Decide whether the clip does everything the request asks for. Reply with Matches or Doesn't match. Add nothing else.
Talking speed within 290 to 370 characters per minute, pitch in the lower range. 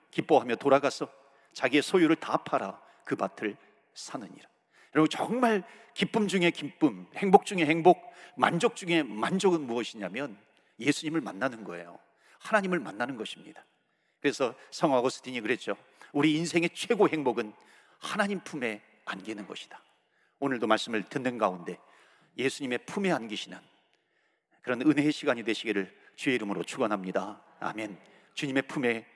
Doesn't match